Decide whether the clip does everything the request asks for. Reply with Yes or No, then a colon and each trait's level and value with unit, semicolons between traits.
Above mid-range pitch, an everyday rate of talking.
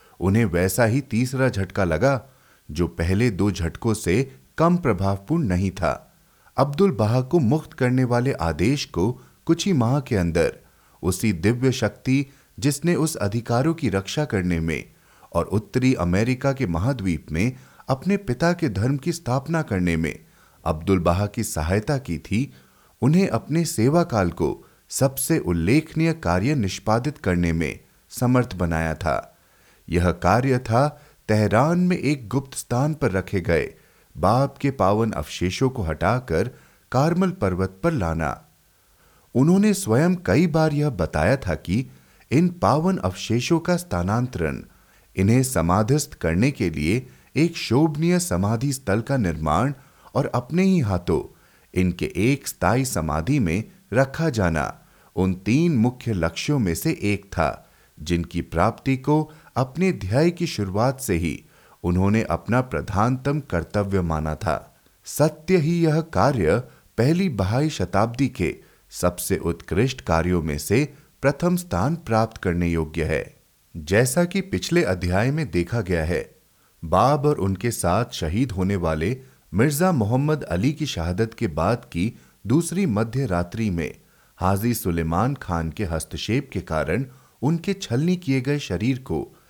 No: low, 115 Hz; average, 140 wpm